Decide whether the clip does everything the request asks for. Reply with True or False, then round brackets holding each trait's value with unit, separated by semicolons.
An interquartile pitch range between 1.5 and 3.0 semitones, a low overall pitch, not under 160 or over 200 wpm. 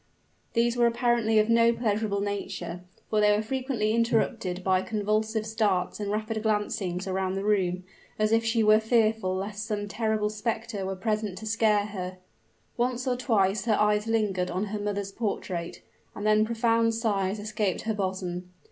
False (2.4 semitones; 215 Hz; 165 wpm)